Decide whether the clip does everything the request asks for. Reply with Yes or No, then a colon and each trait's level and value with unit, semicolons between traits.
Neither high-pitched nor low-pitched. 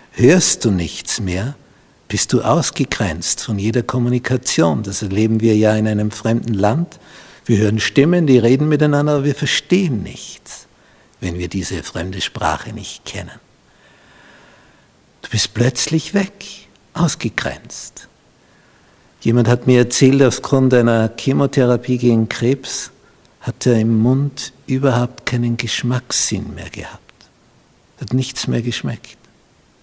No: low, 120 Hz